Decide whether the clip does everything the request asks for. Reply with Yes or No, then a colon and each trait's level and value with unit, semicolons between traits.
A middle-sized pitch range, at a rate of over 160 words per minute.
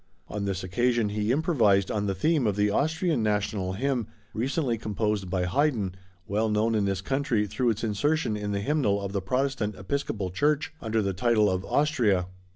Yes: average, 4.7 semitones; average, 180 wpm